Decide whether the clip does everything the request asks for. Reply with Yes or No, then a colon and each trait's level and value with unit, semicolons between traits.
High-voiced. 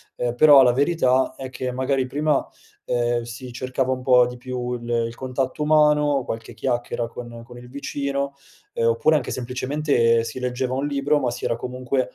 No: low, 130 Hz